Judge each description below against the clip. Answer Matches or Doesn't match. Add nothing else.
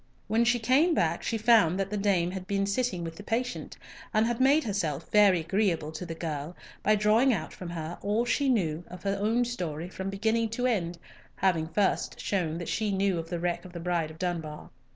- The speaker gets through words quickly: Matches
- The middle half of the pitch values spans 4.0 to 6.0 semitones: Matches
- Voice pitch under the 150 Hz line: Doesn't match